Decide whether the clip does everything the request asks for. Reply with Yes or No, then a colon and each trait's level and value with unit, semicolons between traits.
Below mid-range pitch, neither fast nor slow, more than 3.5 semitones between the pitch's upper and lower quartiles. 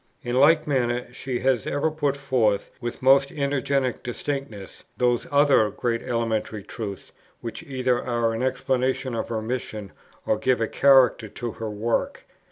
No: low, 125 Hz; average, 155 wpm; average, 3.1 semitones